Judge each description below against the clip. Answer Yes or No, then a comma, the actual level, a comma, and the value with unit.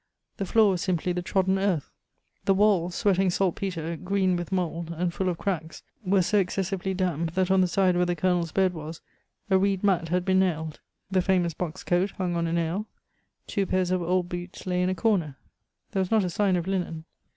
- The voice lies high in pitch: No, medium, 180 Hz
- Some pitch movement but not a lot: No, narrow, 1.9 semitones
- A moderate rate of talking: No, fast, 215 wpm